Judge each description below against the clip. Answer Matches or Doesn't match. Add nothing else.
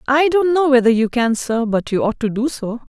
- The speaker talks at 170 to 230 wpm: Doesn't match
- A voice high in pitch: Matches